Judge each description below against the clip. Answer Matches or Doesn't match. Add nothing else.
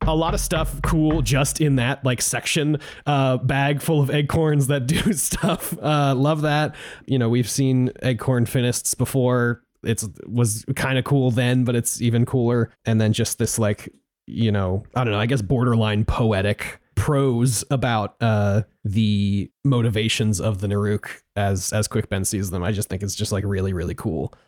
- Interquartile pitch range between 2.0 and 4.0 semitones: Doesn't match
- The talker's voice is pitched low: Matches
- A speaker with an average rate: Matches